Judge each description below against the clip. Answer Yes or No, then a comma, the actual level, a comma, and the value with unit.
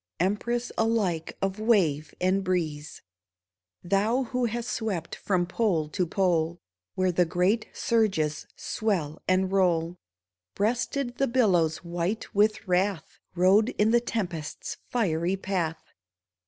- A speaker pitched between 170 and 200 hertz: Yes, high, 190 Hz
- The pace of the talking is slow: Yes, slow, 120 wpm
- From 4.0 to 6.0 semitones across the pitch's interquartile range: Yes, average, 4.4 semitones